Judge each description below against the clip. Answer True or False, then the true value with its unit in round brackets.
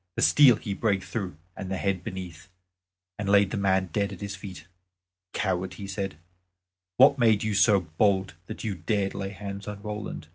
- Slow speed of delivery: False (185 wpm)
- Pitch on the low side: True (100 Hz)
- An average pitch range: False (1.7 semitones)